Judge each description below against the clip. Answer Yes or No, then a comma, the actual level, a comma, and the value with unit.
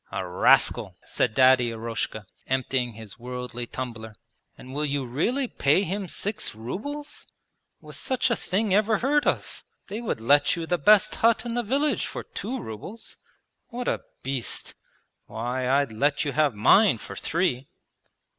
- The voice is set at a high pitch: No, medium, 145 Hz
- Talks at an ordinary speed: Yes, average, 155 wpm